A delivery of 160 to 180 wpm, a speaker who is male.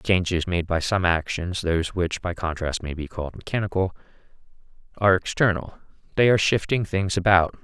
Yes: average, 165 wpm; male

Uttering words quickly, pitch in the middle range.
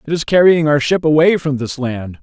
Yes: fast, 245 wpm; medium, 145 Hz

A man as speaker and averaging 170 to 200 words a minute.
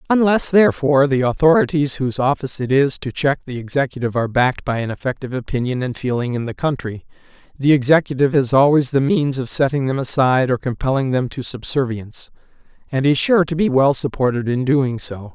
Yes: male; average, 190 wpm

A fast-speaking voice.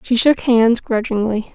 No: average, 155 wpm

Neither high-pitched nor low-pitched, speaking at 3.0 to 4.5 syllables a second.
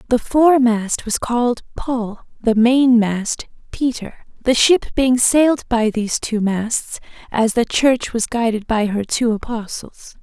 No: high, 235 Hz; 4.1 syllables/s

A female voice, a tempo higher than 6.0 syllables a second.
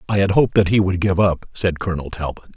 No: male; 6.7 syllables/s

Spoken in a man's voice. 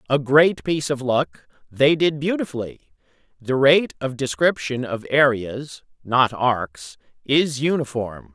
Yes: male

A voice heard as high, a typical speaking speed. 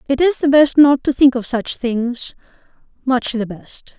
Yes: very high, 260 Hz; average, 180 wpm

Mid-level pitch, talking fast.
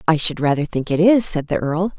Yes: medium, 160 Hz; fast, 270 wpm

